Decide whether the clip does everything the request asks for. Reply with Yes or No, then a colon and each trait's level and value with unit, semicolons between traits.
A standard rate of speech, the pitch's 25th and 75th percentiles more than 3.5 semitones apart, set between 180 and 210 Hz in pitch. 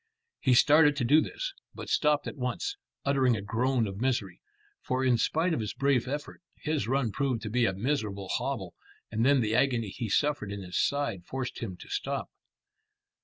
No: average, 190 wpm; average, 4.6 semitones; low, 125 Hz